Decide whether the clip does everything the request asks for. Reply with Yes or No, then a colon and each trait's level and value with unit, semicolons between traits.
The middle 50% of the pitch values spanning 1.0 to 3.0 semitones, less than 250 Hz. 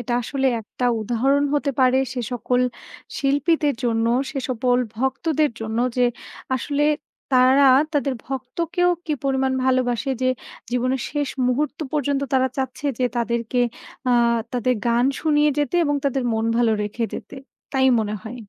No: narrow, 2.6 semitones; very high, 260 Hz